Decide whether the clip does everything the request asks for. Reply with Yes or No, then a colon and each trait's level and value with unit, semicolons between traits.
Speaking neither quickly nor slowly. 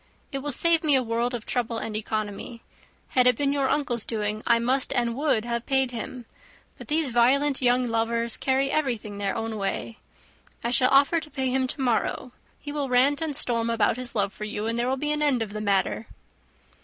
No: fast, 215 wpm